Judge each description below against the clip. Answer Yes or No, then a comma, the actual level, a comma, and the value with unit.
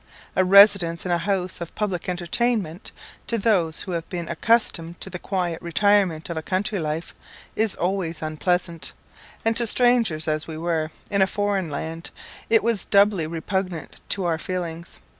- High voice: No, medium, 180 Hz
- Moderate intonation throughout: Yes, average, 3.5 semitones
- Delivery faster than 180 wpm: No, average, 170 wpm